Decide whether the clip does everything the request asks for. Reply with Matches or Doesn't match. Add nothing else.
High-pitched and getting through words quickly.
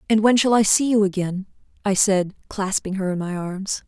Matches